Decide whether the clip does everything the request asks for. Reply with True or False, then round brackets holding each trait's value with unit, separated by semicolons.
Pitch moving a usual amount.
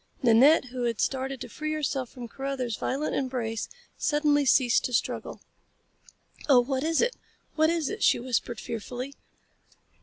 True (3.1 semitones)